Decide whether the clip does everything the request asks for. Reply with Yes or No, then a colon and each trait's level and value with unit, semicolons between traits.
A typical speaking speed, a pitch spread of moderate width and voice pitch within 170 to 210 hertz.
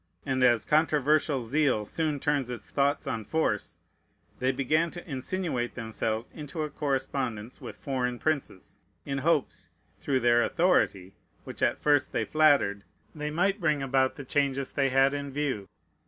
No: average, 155 wpm; average, 3.4 semitones; medium, 140 Hz